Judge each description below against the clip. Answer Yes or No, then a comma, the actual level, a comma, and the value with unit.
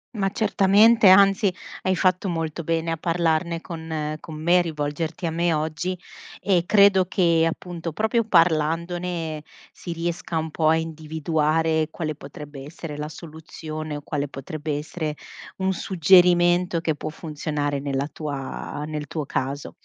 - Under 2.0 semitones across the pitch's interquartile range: No, narrow, 2.5 semitones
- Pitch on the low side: No, medium, 165 Hz